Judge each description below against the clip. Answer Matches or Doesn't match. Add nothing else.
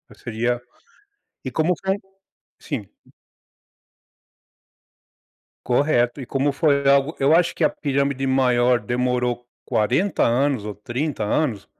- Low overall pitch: Matches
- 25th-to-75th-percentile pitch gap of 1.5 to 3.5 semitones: Matches